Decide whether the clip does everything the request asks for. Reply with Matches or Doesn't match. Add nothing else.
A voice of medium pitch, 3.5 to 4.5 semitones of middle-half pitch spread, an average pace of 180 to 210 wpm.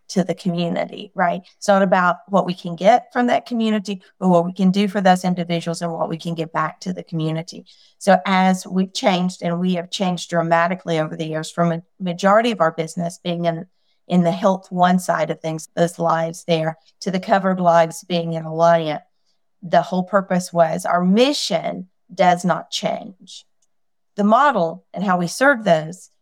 Doesn't match